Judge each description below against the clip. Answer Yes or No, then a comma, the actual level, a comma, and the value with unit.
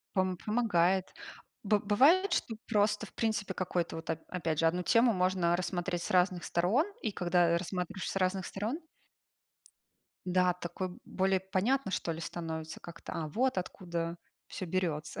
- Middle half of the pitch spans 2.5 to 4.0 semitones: Yes, average, 3.1 semitones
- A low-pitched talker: No, medium, 185 Hz